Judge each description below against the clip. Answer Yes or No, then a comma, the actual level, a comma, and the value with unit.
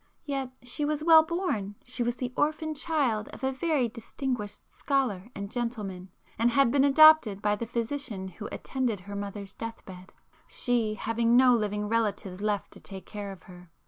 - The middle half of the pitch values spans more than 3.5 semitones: Yes, average, 4.8 semitones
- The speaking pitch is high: Yes, high, 230 Hz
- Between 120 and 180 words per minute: Yes, average, 175 wpm